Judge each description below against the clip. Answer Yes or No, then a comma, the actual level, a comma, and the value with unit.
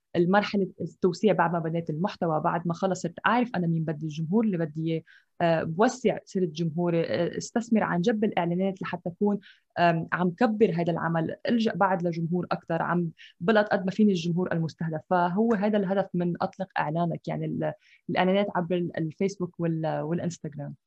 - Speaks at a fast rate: Yes, fast, 150 wpm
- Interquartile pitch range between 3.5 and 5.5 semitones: No, average, 2.8 semitones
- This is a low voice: No, medium, 175 Hz